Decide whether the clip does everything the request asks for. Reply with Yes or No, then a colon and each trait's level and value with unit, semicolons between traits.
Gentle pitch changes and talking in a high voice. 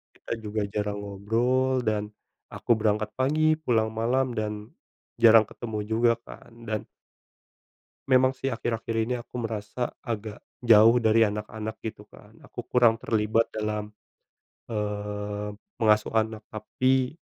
No: narrow, 2.2 semitones; low, 110 Hz